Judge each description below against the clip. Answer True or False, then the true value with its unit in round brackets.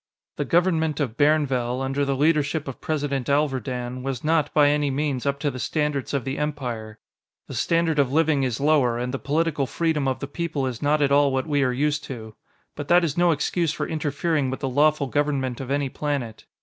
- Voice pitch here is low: False (145 Hz)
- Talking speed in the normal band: False (210 wpm)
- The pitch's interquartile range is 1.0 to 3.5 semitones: True (2.4 semitones)